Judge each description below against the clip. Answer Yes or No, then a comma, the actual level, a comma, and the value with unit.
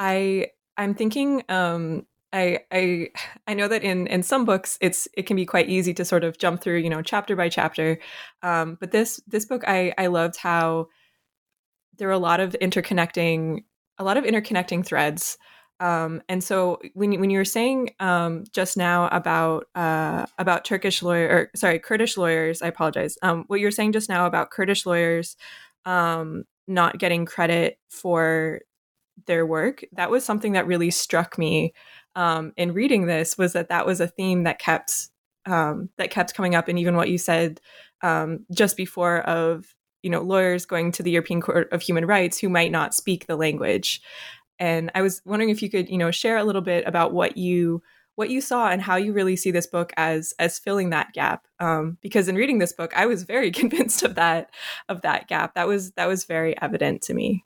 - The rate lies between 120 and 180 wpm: No, average, 200 wpm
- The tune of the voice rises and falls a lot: No, narrow, 2.6 semitones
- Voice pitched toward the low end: No, medium, 180 Hz